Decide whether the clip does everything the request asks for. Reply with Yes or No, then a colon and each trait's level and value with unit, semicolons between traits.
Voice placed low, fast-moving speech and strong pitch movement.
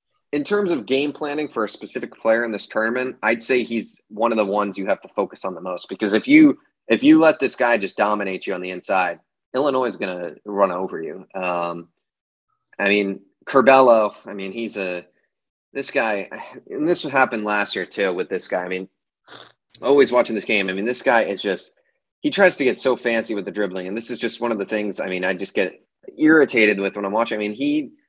Yes: low, 110 Hz; fast, 230 wpm; wide, 5.7 semitones